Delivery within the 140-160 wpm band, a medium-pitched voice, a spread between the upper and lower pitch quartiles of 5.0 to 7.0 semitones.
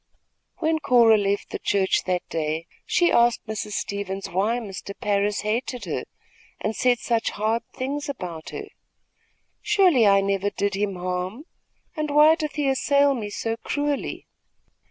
No: average, 150 wpm; high, 220 Hz; wide, 5.4 semitones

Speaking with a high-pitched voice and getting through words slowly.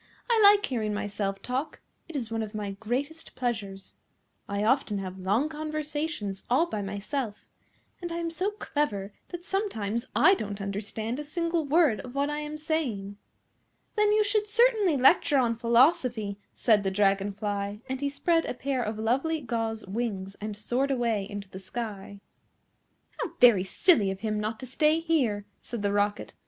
No: high, 235 Hz; average, 170 wpm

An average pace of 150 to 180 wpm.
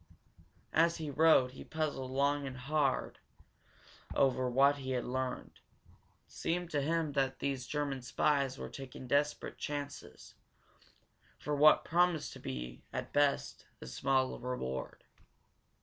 No: slow, 135 wpm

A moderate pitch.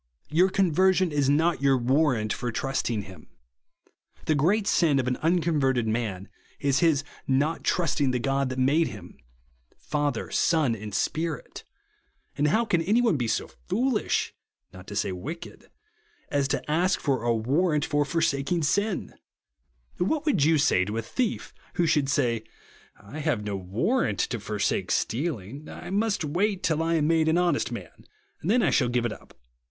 Yes: medium, 145 Hz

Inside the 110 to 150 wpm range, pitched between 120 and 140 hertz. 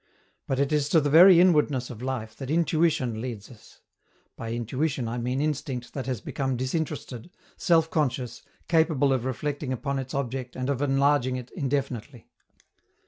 No: average, 160 wpm; low, 135 Hz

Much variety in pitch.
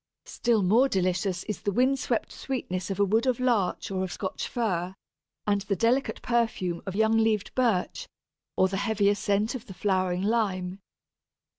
No: average, 3.7 semitones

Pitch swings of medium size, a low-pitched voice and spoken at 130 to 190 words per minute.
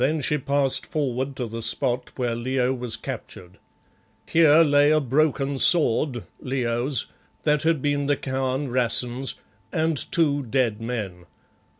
Yes: average, 3.1 semitones; low, 130 Hz; slow, 135 wpm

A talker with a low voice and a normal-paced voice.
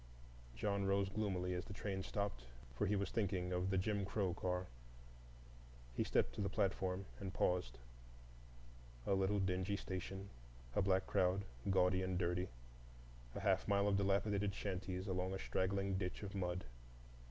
Yes: very low, 95 Hz; average, 155 wpm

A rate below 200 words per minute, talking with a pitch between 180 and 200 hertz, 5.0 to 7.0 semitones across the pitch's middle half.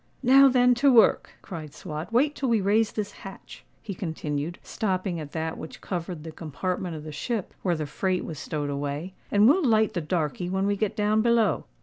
No: fast, 205 wpm; medium, 185 Hz; wide, 5.6 semitones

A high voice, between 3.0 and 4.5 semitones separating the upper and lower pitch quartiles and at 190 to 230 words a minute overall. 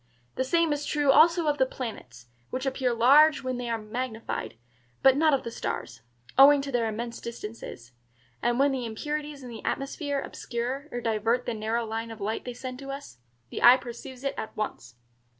Yes: very high, 250 Hz; average, 3.4 semitones; average, 195 wpm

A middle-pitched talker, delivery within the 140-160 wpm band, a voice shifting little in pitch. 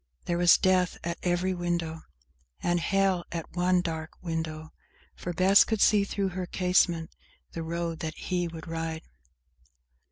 Yes: medium, 175 Hz; average, 150 wpm; narrow, 1.9 semitones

